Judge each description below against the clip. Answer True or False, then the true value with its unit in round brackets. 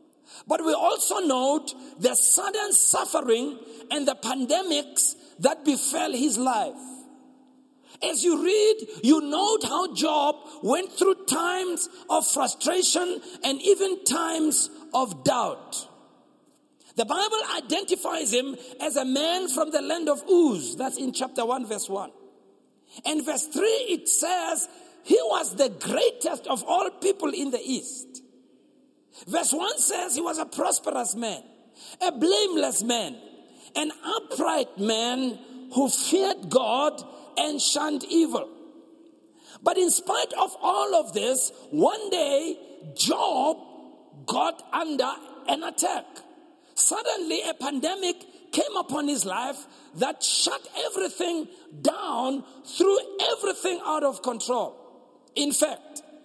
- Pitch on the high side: True (310 Hz)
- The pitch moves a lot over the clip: False (4.6 semitones)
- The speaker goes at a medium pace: False (125 wpm)